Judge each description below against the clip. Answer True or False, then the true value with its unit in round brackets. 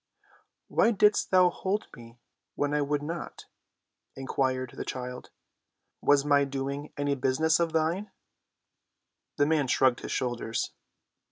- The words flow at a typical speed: False (125 wpm)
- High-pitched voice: False (145 Hz)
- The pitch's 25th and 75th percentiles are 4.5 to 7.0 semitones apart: False (3.6 semitones)